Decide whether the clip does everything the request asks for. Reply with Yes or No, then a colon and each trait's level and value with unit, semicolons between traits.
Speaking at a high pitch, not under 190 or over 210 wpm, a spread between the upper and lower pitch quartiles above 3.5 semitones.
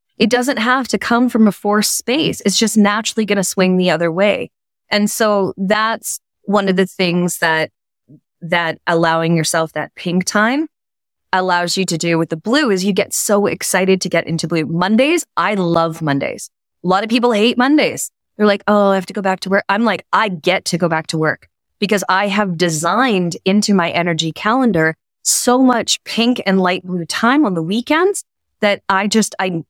Yes: high, 195 Hz; average, 200 wpm; average, 4.2 semitones